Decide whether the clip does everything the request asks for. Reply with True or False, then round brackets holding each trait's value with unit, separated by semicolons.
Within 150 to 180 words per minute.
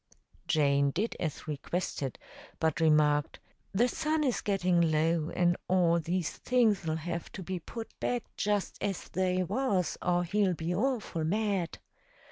False (140 wpm)